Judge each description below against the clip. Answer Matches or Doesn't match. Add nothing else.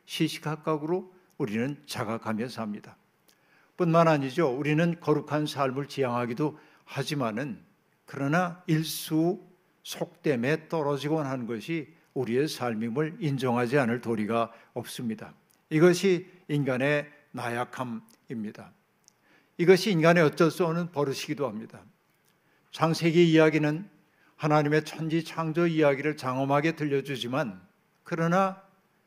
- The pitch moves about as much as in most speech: Matches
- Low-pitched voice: Doesn't match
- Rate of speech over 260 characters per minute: Matches